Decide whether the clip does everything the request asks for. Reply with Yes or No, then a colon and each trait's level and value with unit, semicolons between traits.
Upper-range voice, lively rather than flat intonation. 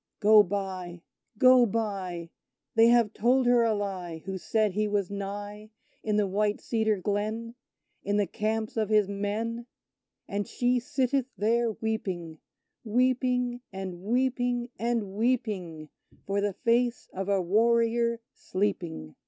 No: high, 215 Hz; average, 3.1 semitones